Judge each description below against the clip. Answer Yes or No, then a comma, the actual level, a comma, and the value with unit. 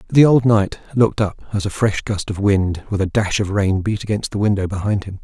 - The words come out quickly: Yes, fast, 250 wpm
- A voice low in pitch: Yes, low, 100 Hz